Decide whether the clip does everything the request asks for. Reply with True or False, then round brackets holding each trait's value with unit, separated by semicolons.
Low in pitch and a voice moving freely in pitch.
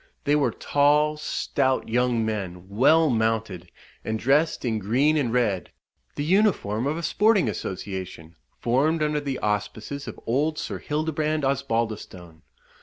True (130 Hz; 5.8 semitones)